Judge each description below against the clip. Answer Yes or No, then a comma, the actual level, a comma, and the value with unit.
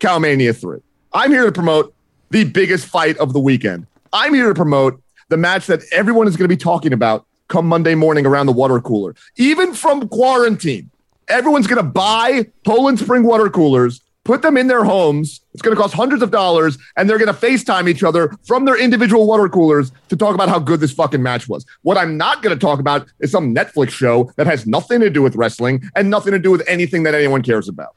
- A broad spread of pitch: Yes, wide, 8.0 semitones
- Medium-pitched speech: Yes, medium, 170 Hz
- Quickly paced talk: Yes, fast, 225 wpm